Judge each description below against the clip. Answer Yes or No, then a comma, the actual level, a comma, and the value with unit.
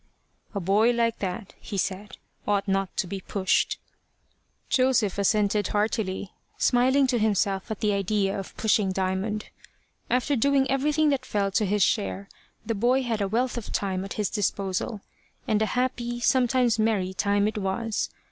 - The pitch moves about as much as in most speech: Yes, average, 3.4 semitones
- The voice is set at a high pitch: Yes, high, 210 Hz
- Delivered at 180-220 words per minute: No, average, 165 wpm